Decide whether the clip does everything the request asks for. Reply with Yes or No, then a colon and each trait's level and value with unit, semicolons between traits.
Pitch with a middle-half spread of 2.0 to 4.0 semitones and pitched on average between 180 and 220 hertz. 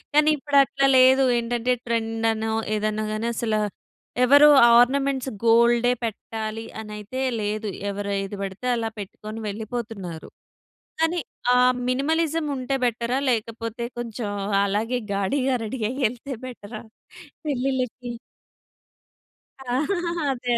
No: average, 3.1 semitones; high, 235 Hz